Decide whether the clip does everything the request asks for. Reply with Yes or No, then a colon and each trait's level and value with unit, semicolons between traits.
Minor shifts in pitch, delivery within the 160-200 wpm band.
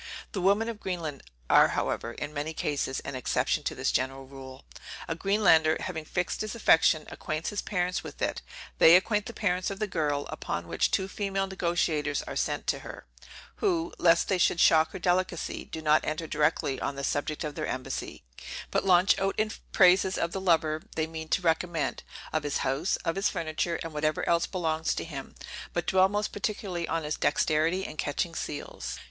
No: average, 3.7 semitones; average, 190 wpm